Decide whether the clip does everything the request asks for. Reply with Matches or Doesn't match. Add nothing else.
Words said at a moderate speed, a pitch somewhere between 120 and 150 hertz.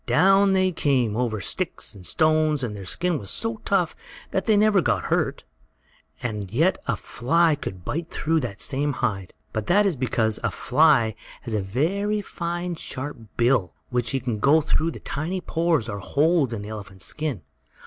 Matches